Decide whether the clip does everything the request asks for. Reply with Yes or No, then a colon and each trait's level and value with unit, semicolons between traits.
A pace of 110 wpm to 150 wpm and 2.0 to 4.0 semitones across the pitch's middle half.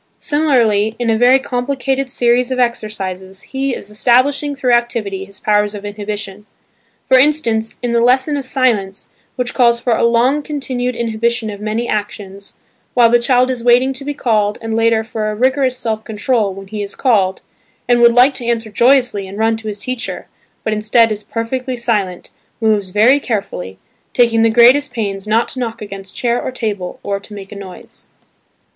No: average, 185 wpm; average, 3.3 semitones